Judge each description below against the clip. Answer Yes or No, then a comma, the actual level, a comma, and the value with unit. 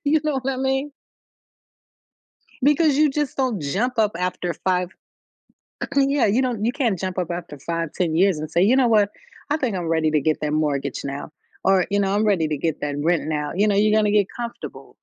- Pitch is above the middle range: Yes, high, 200 Hz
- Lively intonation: Yes, wide, 7.4 semitones